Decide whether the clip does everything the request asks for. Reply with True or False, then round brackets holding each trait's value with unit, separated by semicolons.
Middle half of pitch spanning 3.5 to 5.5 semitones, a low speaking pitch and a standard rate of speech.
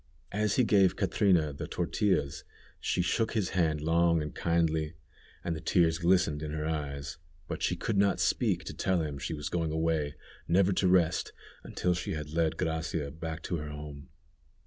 False (3.0 semitones; 80 Hz; 180 wpm)